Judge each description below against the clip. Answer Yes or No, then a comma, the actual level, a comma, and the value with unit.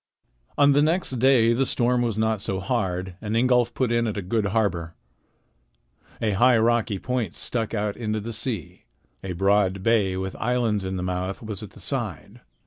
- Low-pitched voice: Yes, low, 110 Hz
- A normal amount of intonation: Yes, average, 3.6 semitones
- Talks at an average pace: Yes, average, 185 wpm